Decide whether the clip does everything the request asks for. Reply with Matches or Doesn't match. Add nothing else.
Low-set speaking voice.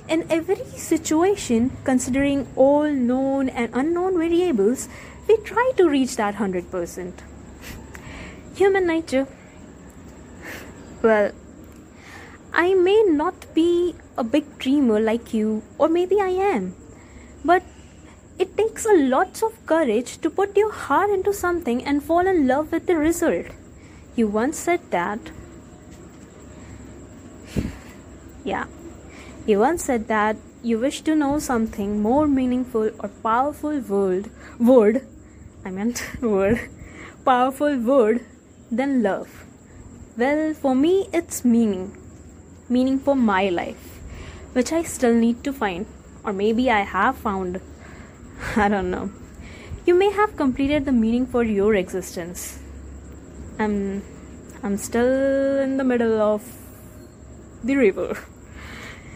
Doesn't match